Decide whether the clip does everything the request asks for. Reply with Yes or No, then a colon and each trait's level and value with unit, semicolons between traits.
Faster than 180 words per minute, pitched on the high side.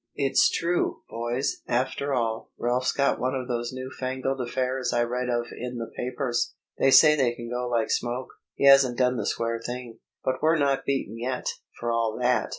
No: average, 190 wpm; low, 125 Hz